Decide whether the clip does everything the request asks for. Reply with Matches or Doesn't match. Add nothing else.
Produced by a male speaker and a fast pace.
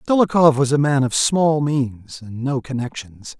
Doesn't match